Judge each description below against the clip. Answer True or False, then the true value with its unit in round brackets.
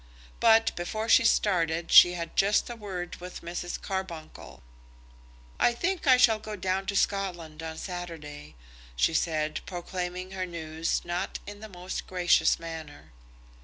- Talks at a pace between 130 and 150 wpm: True (145 wpm)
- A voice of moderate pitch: True (180 Hz)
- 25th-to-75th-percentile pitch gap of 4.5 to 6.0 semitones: False (3.3 semitones)